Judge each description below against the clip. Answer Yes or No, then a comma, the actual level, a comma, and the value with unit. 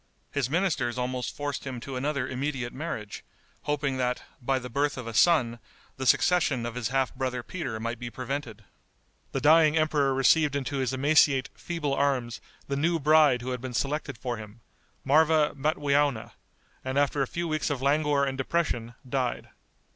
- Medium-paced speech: Yes, average, 170 wpm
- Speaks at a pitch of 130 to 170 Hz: Yes, low, 135 Hz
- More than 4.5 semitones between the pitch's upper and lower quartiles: No, average, 2.9 semitones